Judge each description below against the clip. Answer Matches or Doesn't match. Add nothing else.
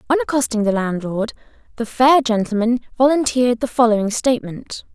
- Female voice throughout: Matches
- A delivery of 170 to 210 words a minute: Doesn't match